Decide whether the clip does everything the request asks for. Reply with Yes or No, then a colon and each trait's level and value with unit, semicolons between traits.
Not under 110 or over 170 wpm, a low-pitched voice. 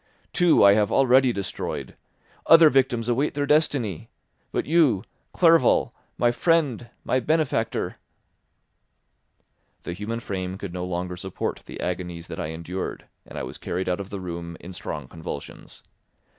Yes: average, 145 wpm; low, 105 Hz